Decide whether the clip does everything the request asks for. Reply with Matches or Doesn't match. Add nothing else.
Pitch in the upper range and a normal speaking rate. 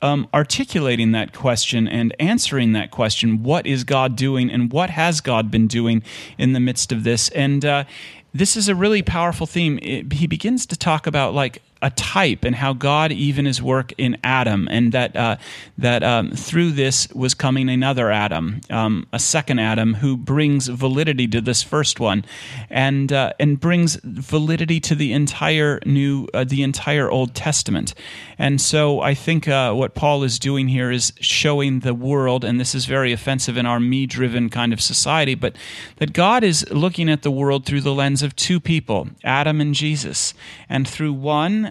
Doesn't match